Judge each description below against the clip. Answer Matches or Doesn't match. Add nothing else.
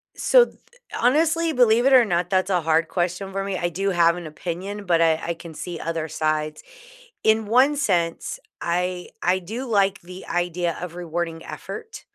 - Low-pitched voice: Doesn't match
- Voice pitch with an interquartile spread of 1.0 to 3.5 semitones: Doesn't match